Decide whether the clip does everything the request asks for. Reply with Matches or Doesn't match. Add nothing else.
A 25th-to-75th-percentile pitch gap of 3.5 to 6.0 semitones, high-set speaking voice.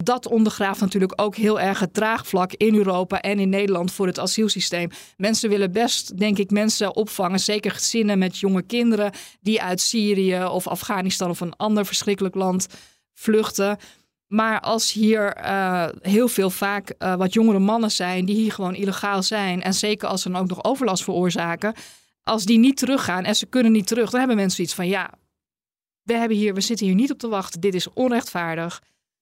Doesn't match